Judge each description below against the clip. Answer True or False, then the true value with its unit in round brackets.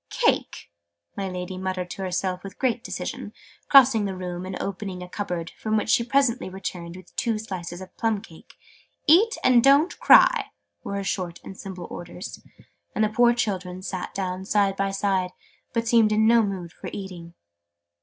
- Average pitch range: True (3.6 semitones)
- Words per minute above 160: True (175 wpm)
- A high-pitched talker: True (195 Hz)